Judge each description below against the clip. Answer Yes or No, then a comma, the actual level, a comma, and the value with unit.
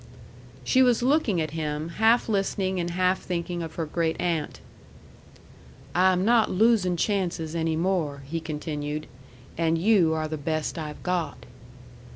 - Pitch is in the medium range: Yes, medium, 170 Hz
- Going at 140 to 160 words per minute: Yes, average, 150 wpm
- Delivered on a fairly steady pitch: No, average, 3.2 semitones